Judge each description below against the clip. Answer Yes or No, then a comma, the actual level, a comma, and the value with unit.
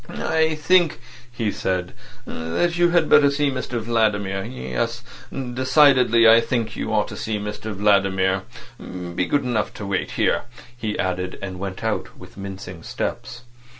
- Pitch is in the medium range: No, low, 110 Hz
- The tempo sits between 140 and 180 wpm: Yes, average, 150 wpm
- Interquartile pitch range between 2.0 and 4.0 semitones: No, average, 5.2 semitones